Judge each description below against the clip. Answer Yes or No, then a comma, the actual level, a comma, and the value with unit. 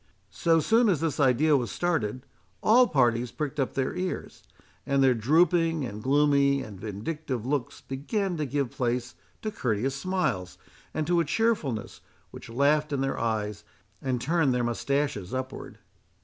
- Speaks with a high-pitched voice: No, medium, 140 Hz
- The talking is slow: No, average, 155 wpm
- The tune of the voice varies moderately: Yes, average, 4.7 semitones